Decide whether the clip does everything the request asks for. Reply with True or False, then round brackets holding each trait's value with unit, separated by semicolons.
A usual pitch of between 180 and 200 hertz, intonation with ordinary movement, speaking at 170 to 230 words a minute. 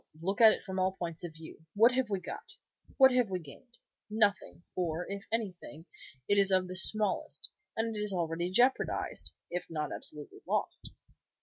True (190 Hz; 4.1 semitones; 180 wpm)